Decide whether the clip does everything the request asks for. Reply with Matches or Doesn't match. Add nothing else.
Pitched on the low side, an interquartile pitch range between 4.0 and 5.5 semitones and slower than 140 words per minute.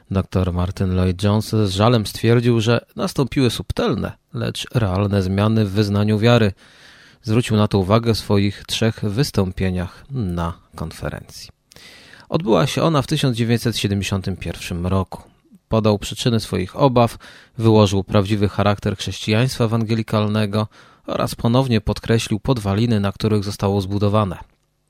Doesn't match